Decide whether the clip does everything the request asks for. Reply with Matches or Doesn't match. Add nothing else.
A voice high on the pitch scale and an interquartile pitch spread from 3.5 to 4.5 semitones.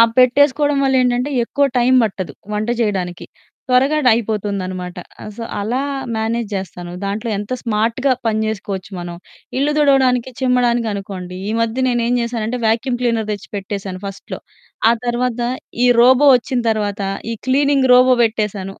Matches